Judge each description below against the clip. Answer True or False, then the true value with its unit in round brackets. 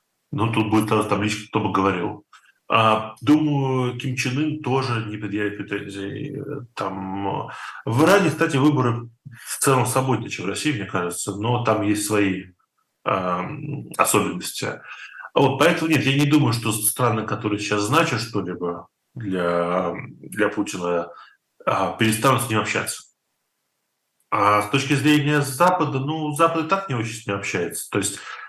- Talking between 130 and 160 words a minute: True (145 wpm)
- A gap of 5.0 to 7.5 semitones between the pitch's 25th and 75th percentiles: True (5.5 semitones)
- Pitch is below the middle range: True (115 Hz)